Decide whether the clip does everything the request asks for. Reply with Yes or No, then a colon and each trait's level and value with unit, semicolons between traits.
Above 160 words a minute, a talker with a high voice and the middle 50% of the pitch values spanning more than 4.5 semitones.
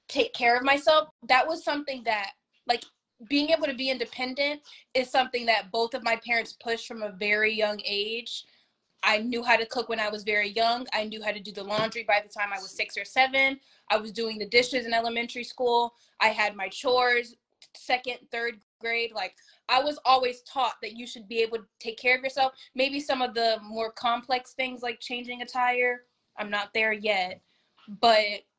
No: fast, 205 wpm; high, 235 Hz; average, 2.9 semitones